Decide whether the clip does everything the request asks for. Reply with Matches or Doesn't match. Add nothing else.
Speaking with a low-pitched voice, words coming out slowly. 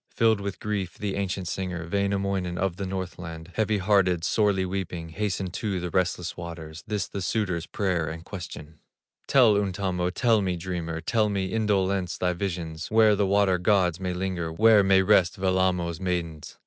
Doesn't match